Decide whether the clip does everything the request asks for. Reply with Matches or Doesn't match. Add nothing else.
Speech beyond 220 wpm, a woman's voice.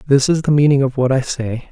Doesn't match